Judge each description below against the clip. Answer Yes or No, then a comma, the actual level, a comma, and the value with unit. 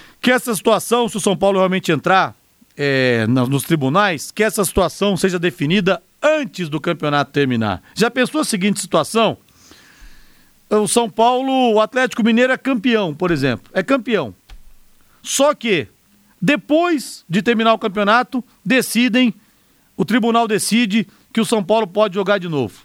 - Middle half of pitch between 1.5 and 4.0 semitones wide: No, average, 4.9 semitones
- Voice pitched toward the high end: Yes, high, 210 Hz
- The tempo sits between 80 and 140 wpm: No, average, 150 wpm